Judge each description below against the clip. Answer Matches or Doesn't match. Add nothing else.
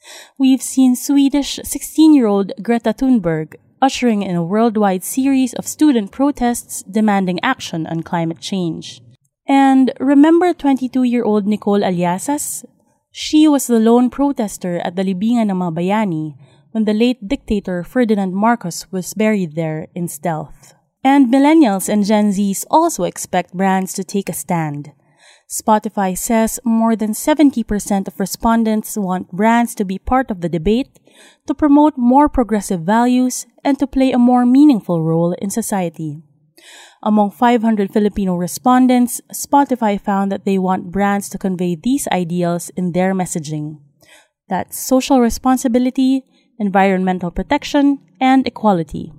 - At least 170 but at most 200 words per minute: Doesn't match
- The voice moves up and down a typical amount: Doesn't match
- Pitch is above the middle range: Matches